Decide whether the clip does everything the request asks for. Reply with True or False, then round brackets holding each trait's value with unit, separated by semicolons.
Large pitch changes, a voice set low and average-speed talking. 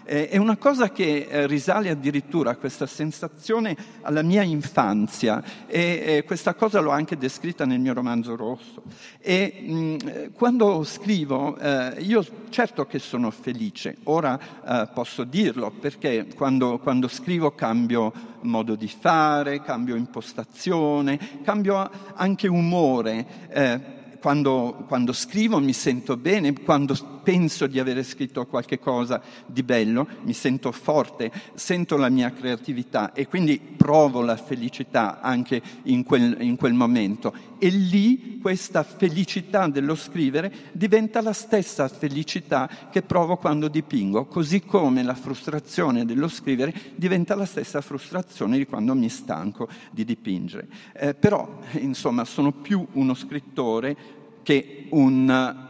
False (7.1 semitones; 155 Hz; 135 wpm)